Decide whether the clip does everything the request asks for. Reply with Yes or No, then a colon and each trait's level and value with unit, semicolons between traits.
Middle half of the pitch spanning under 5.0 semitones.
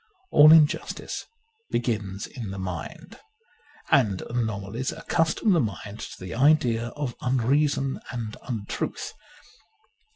No: wide, 5.4 semitones